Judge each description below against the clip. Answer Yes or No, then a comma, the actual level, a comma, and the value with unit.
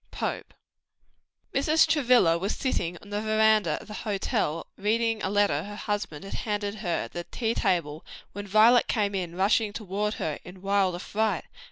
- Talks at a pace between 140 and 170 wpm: Yes, average, 165 wpm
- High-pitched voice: Yes, high, 205 Hz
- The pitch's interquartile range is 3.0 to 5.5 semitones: No, narrow, 2.5 semitones